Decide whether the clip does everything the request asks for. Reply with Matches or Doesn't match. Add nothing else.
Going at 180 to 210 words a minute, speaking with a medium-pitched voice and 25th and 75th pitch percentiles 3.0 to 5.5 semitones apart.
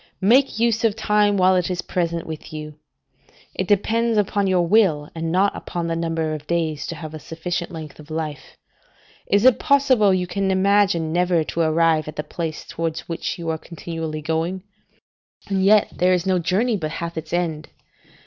Matches